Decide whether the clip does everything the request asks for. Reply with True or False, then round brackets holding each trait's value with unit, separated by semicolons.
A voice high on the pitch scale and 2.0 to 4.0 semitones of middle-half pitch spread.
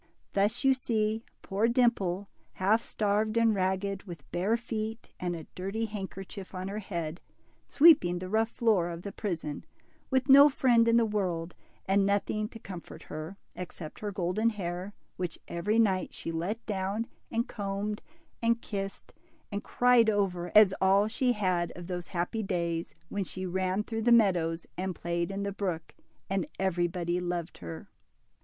True (195 Hz; 3.6 semitones)